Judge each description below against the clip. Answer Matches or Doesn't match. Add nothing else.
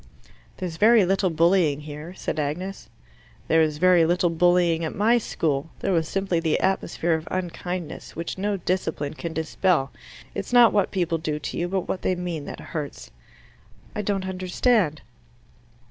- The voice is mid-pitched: Matches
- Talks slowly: Doesn't match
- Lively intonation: Doesn't match